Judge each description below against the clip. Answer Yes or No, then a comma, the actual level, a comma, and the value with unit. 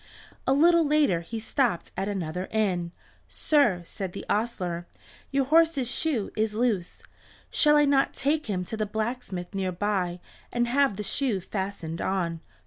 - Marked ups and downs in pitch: Yes, wide, 6.8 semitones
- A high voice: Yes, high, 215 Hz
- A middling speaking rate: Yes, average, 155 wpm